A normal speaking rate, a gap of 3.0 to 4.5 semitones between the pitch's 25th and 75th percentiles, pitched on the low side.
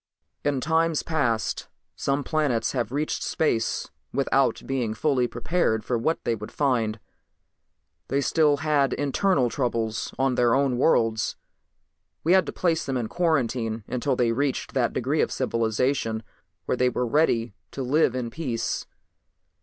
Yes: average, 145 wpm; average, 3.9 semitones; low, 130 Hz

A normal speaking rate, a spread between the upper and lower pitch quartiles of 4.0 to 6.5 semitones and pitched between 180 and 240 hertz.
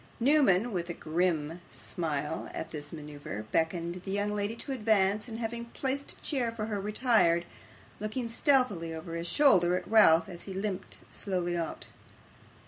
Yes: average, 160 wpm; average, 5.2 semitones; high, 190 Hz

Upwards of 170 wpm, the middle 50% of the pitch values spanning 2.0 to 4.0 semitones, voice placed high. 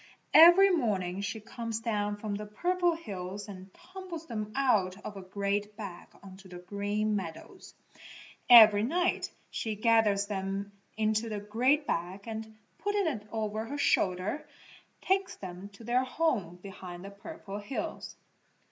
No: average, 145 wpm; average, 3.7 semitones; high, 210 Hz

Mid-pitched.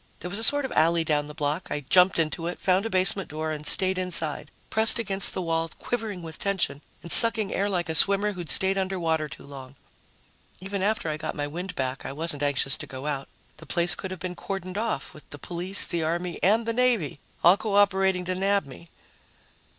Yes: medium, 180 Hz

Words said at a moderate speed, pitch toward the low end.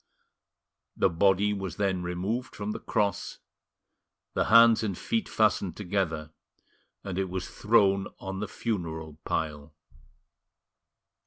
No: slow, 115 wpm; very low, 95 Hz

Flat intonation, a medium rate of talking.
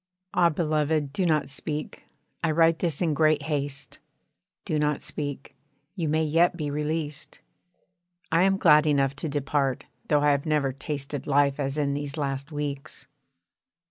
Yes: narrow, 1.9 semitones; average, 155 wpm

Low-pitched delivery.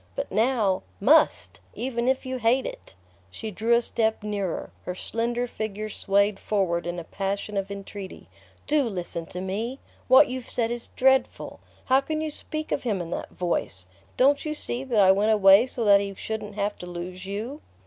No: high, 215 Hz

